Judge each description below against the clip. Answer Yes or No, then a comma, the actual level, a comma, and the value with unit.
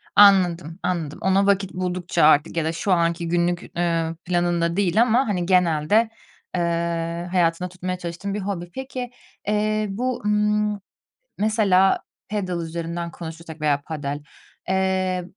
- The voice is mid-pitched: Yes, medium, 180 Hz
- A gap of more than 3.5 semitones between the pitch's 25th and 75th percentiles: No, average, 3.1 semitones